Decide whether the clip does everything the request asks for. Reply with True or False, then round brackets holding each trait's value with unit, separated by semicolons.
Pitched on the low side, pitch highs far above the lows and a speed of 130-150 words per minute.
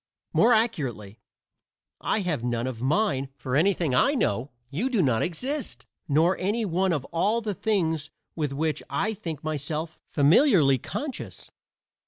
False (160 Hz; 7.2 semitones; 145 wpm)